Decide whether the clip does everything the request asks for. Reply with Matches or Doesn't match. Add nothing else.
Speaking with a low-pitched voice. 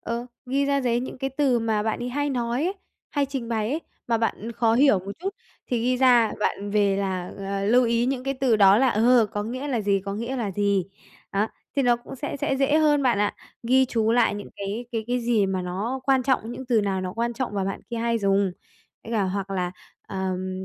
Doesn't match